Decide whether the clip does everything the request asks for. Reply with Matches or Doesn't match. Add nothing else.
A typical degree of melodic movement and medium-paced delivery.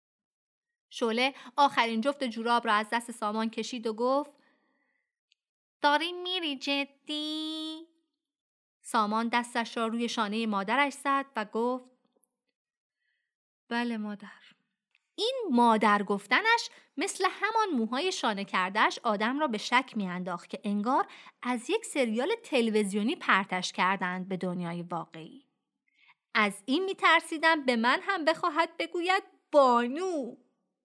Doesn't match